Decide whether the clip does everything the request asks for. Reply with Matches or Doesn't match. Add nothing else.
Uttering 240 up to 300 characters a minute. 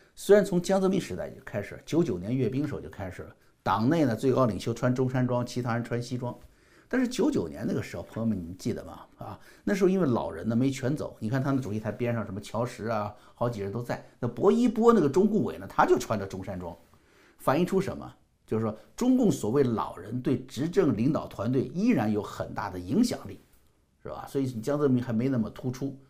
Doesn't match